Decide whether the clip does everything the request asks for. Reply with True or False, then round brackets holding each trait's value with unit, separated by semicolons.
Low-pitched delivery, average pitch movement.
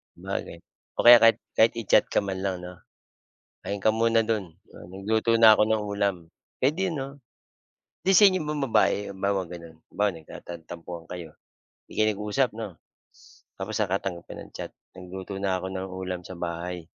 True (100 Hz; 3.5 semitones)